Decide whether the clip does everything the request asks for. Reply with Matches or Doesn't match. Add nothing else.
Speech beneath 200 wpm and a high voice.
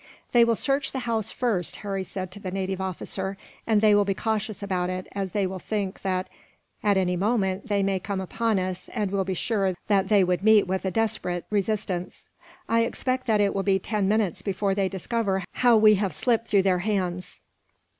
Doesn't match